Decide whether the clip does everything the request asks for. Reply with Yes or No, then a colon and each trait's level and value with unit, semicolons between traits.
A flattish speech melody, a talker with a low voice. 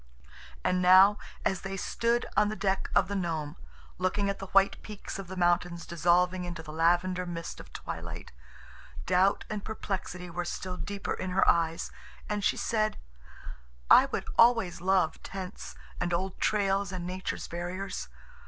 No: narrow, 2.1 semitones; medium, 185 Hz